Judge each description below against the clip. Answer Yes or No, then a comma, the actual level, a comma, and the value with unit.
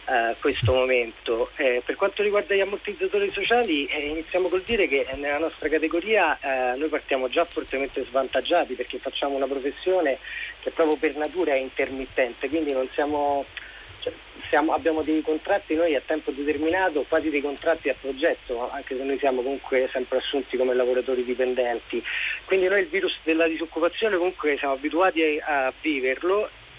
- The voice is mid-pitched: Yes, medium, 155 Hz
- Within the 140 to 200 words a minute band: Yes, average, 165 wpm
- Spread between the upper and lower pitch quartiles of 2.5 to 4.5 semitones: No, average, 5.0 semitones